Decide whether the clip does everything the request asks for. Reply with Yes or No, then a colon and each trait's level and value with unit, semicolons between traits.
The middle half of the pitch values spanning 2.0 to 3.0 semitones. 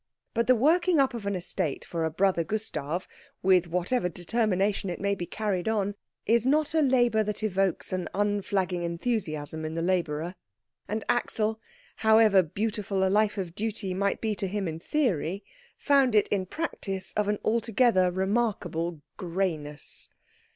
No: average, 3.7 semitones